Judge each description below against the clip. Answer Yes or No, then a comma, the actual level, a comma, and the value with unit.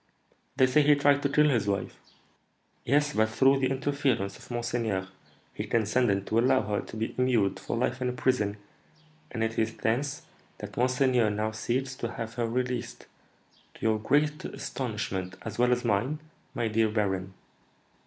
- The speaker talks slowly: No, average, 170 wpm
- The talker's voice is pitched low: Yes, low, 120 Hz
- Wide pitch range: No, average, 3.3 semitones